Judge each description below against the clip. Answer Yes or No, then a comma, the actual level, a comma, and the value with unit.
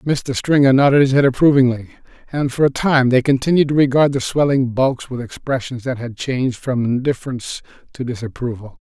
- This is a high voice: No, low, 130 Hz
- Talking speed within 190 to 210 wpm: No, average, 175 wpm